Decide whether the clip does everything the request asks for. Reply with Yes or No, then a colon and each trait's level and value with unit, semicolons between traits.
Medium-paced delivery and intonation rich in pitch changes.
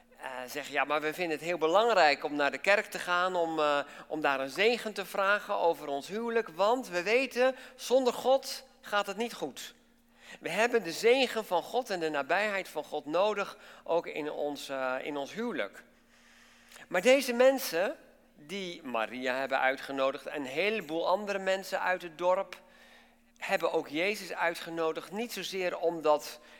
Yes: average, 170 wpm; wide, 7.5 semitones